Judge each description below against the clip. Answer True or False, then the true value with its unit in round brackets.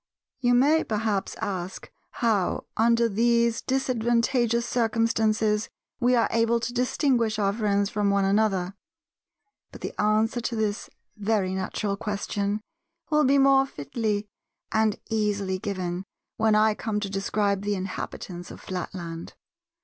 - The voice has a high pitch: True (215 Hz)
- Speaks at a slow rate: True (130 wpm)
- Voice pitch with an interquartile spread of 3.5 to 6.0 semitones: False (2.7 semitones)